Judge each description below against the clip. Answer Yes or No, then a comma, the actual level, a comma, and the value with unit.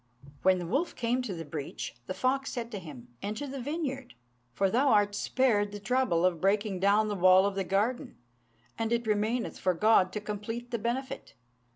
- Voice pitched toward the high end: Yes, high, 210 Hz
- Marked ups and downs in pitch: No, average, 4.5 semitones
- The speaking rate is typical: Yes, average, 195 wpm